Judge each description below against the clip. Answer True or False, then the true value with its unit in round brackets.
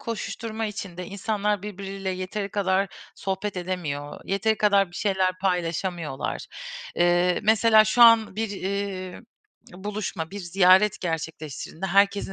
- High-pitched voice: True (195 Hz)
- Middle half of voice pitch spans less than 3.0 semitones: True (2.5 semitones)